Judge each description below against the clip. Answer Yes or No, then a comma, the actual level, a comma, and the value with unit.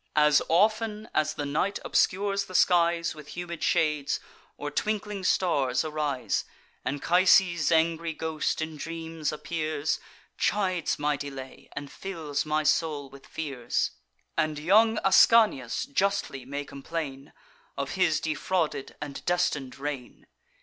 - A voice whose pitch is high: No, medium, 155 Hz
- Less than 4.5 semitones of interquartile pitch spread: Yes, average, 3.7 semitones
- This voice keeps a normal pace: No, slow, 120 wpm